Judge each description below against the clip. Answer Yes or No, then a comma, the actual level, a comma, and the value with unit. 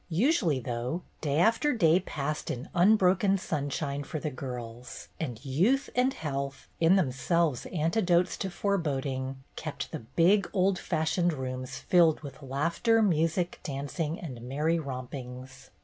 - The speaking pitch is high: No, medium, 155 Hz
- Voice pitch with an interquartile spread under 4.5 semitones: No, average, 5.1 semitones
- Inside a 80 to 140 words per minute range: Yes, slow, 135 wpm